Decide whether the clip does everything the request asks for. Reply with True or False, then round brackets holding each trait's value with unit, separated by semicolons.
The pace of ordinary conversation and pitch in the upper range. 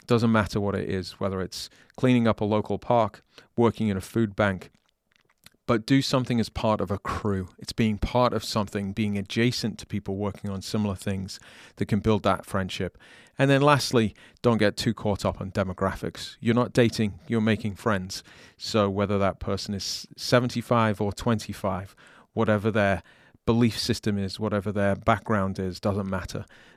False (175 wpm; 105 Hz)